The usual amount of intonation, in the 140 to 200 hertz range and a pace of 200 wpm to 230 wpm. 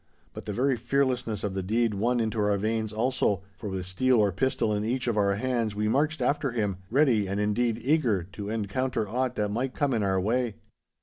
No: average, 3.6 semitones; low, 110 Hz; fast, 205 wpm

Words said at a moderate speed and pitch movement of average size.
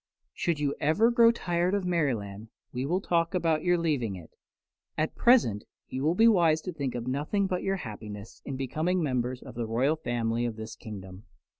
No: average, 190 wpm; wide, 7.2 semitones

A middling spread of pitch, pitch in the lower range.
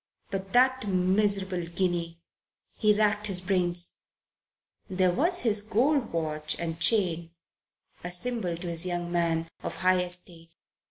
No: average, 3.3 semitones; medium, 180 Hz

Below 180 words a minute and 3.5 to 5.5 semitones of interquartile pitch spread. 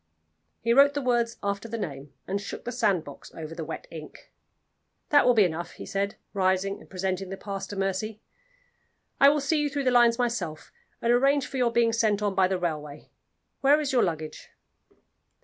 No: average, 195 wpm; average, 4.8 semitones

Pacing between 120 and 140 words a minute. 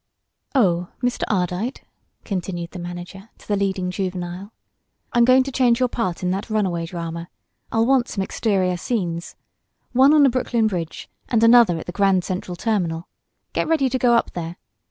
No: average, 175 wpm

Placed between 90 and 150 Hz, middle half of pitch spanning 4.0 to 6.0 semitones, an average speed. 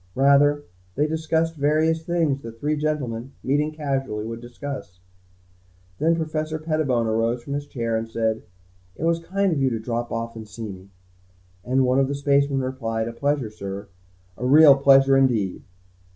Yes: low, 135 Hz; average, 4.7 semitones; average, 165 wpm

